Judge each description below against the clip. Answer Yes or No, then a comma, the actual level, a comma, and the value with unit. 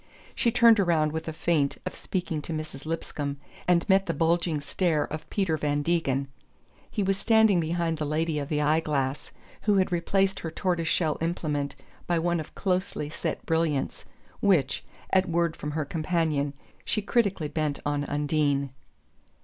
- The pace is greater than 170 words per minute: No, average, 165 wpm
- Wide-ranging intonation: No, average, 3.0 semitones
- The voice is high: No, medium, 160 Hz